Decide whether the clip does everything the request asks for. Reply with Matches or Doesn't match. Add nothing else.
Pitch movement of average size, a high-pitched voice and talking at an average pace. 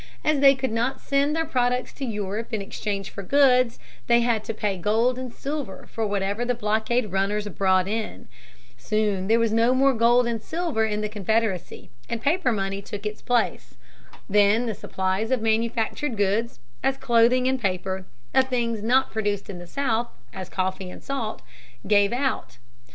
Matches